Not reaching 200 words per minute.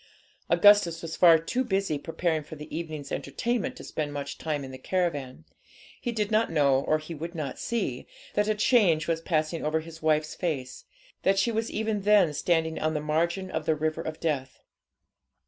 Yes: average, 190 wpm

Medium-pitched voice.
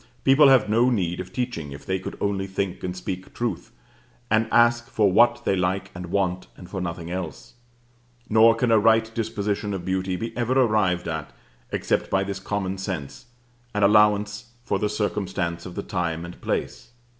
No: low, 100 Hz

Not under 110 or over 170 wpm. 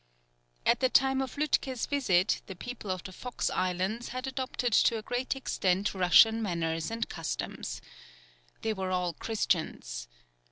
Yes: average, 150 wpm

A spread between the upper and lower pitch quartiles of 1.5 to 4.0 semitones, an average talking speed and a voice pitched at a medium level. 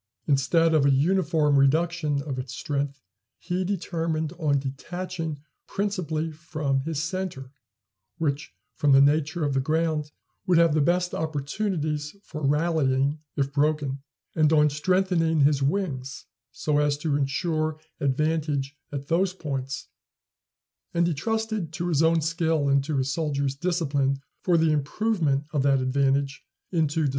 Yes: average, 2.9 semitones; average, 145 wpm; medium, 150 Hz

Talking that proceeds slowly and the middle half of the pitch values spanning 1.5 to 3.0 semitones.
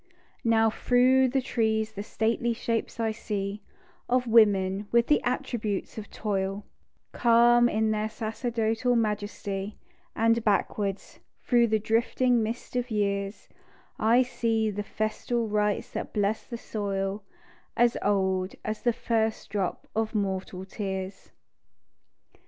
Yes: slow, 125 wpm; narrow, 2.5 semitones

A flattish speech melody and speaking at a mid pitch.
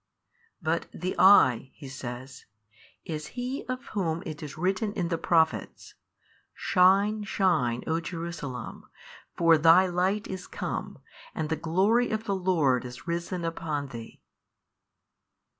No: average, 4.0 semitones; medium, 170 Hz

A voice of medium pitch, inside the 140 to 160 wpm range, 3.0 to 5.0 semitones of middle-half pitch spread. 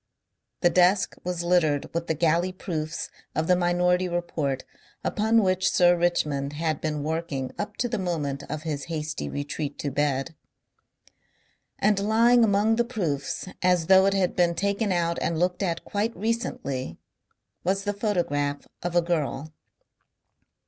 Yes: medium, 175 Hz; average, 150 wpm; average, 4.1 semitones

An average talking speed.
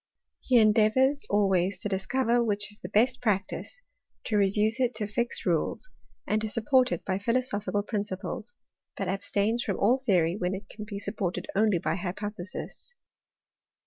Yes: average, 155 wpm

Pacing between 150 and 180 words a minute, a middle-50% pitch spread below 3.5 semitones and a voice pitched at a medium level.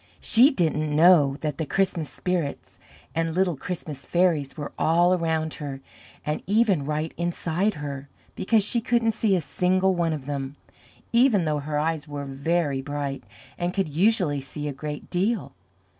No: average, 160 wpm; average, 3.9 semitones; medium, 160 Hz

